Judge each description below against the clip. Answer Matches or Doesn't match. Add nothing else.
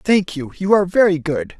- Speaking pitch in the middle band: Matches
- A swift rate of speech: Matches